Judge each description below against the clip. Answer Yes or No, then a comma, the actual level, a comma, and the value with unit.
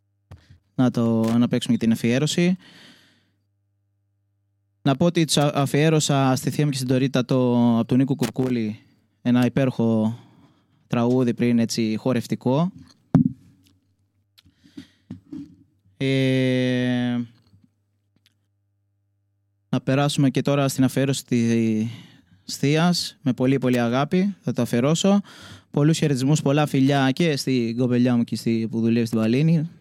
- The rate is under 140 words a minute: Yes, average, 120 wpm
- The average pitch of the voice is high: No, low, 125 Hz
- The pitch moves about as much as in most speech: Yes, average, 4.1 semitones